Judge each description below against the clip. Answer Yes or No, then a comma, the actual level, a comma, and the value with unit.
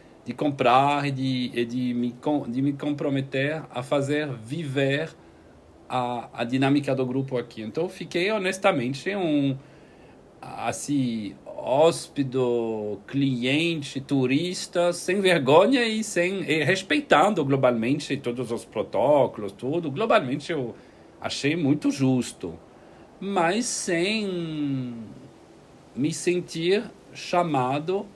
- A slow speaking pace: Yes, slow, 100 wpm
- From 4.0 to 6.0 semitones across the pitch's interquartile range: Yes, average, 5.3 semitones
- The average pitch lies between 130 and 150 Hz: Yes, medium, 140 Hz